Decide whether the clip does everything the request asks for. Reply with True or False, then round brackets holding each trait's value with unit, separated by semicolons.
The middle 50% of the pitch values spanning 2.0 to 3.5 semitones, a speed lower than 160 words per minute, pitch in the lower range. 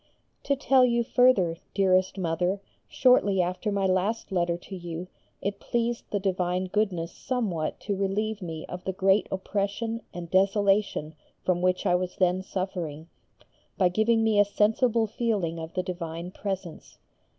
False (3.0 semitones; 150 wpm; 190 Hz)